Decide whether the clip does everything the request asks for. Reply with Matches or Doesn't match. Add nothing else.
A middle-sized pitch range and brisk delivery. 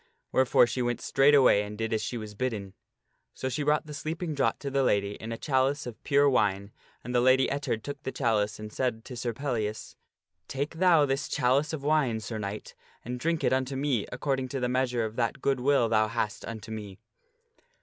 Matches